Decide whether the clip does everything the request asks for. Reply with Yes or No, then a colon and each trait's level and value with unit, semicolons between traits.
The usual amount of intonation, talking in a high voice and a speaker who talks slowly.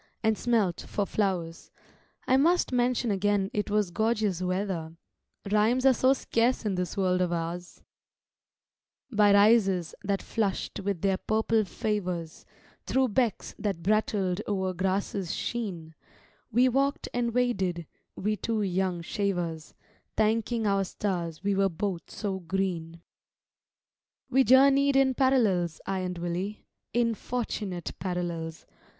Yes: average, 4.1 semitones; high, 200 Hz; slow, 130 wpm